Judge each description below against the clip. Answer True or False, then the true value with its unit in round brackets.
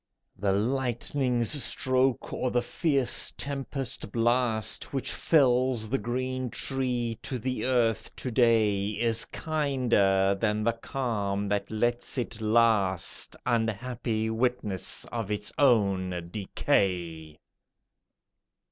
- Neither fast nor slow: False (105 wpm)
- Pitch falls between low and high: False (115 Hz)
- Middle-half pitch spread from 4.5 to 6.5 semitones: False (3.6 semitones)